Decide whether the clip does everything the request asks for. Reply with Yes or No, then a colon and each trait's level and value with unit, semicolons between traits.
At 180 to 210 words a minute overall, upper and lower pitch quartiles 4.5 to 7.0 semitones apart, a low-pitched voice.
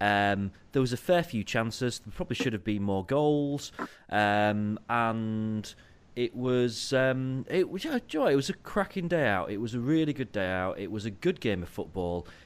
Yes: average, 200 wpm; average, 5.2 semitones; low, 115 Hz